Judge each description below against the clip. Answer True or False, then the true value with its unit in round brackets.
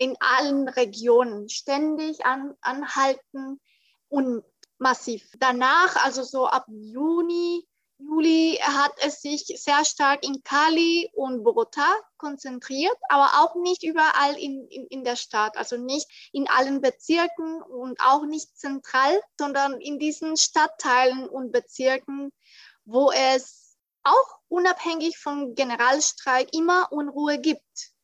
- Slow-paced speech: True (120 wpm)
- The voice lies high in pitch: True (280 Hz)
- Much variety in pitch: False (3.5 semitones)